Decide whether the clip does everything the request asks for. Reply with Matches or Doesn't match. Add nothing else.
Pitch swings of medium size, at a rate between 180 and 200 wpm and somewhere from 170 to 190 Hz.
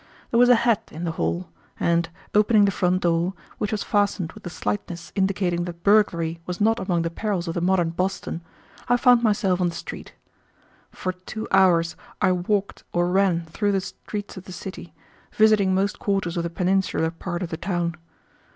Matches